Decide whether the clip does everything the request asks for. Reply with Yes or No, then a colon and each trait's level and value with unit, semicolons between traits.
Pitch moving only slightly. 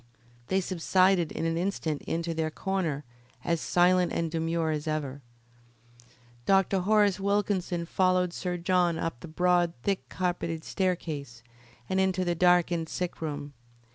Yes: narrow, 2.3 semitones